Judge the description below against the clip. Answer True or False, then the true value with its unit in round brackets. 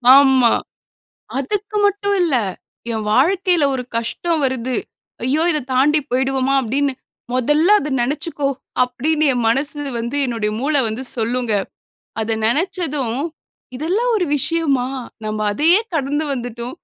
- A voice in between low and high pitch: False (275 Hz)